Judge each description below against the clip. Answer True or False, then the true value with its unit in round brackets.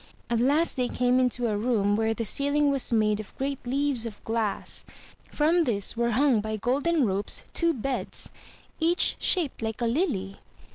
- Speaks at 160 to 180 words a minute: True (175 wpm)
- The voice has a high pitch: True (245 Hz)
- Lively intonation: False (4.5 semitones)